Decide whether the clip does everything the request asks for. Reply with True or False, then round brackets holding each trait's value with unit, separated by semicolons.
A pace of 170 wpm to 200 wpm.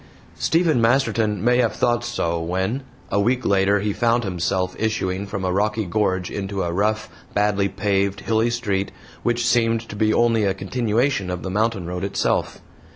True (175 wpm)